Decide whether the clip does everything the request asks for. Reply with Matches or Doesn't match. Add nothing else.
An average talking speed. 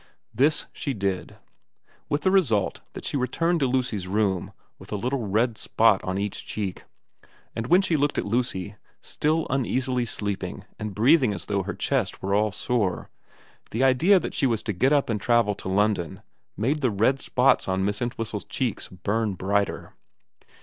Matches